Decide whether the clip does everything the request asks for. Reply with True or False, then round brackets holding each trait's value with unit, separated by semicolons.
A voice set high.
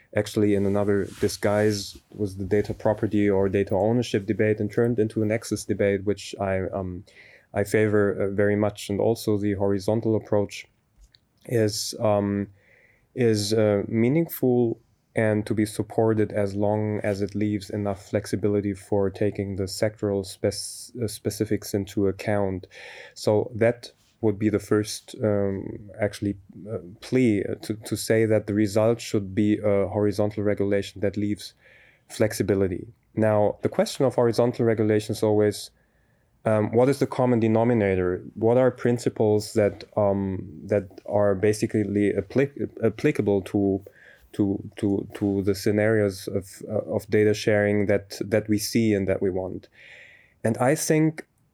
False (105 Hz)